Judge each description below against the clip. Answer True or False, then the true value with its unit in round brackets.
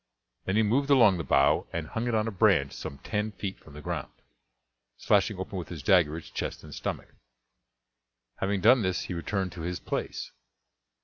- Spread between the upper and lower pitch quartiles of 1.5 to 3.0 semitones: False (4.1 semitones)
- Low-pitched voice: True (95 Hz)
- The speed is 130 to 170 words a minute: False (190 wpm)